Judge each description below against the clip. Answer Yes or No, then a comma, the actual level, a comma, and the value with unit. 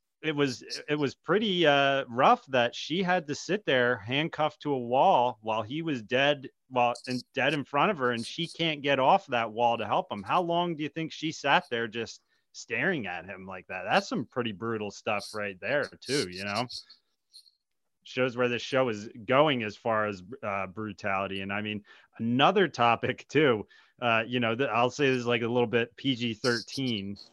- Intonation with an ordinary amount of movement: Yes, average, 4.0 semitones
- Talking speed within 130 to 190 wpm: No, fast, 205 wpm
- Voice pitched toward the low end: Yes, low, 120 Hz